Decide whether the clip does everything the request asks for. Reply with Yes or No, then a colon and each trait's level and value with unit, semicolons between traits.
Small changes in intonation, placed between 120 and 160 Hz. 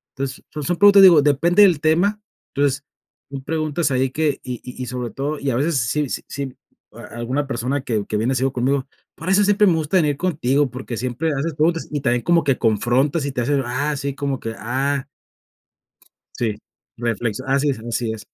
No: average, 3.6 semitones; medium, 140 Hz